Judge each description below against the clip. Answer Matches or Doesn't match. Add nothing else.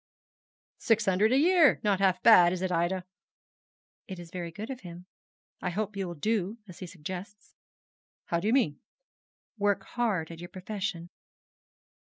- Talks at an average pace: Matches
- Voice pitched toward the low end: Doesn't match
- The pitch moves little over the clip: Doesn't match